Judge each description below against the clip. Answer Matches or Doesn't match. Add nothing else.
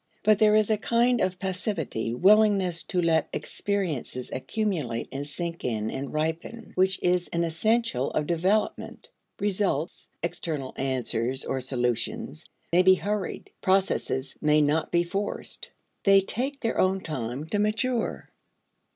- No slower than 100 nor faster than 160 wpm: Matches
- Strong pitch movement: Matches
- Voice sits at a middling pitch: Matches